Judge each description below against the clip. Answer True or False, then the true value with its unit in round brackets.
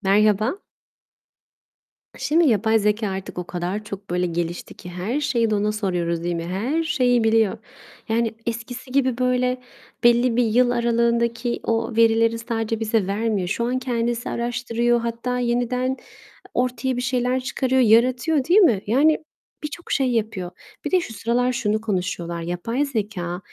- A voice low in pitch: False (230 Hz)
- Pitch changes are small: False (3.1 semitones)